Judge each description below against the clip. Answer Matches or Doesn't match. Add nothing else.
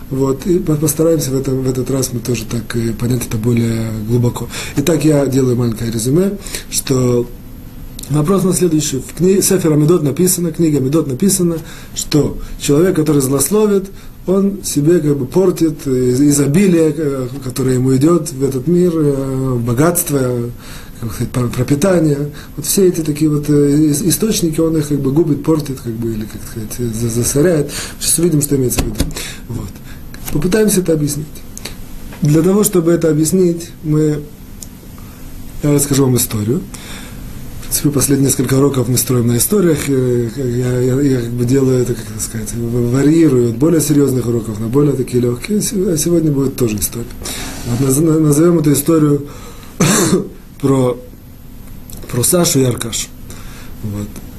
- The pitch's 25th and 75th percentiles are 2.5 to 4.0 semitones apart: Doesn't match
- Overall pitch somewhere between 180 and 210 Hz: Doesn't match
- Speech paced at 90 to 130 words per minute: Doesn't match